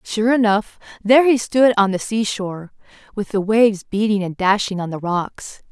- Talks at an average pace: Yes, average, 190 wpm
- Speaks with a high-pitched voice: Yes, high, 210 Hz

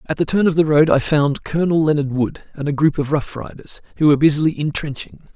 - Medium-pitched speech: Yes, medium, 150 Hz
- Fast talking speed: Yes, fast, 235 wpm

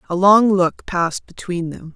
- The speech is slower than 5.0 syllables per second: Yes, 4.5 syllables/s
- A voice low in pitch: No, medium, 185 Hz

